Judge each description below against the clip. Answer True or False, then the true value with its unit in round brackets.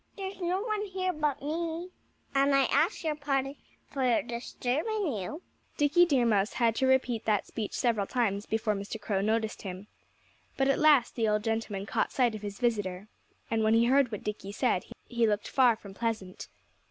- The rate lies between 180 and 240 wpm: True (185 wpm)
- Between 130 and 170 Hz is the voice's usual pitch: False (235 Hz)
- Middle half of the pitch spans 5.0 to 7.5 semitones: True (5.3 semitones)